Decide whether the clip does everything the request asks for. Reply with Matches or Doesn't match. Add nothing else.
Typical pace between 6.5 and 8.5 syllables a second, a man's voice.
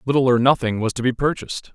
Matches